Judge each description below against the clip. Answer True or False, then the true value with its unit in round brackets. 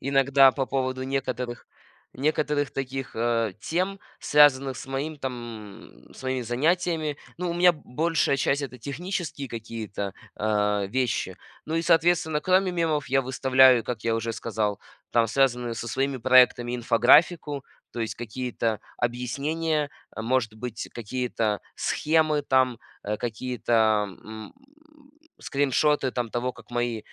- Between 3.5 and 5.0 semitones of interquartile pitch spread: True (3.9 semitones)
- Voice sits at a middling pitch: False (130 Hz)